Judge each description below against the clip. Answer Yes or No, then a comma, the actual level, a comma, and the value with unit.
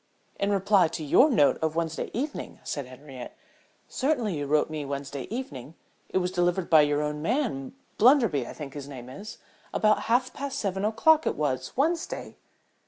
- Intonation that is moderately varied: No, wide, 7.8 semitones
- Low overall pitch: No, medium, 170 Hz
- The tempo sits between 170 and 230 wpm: Yes, average, 175 wpm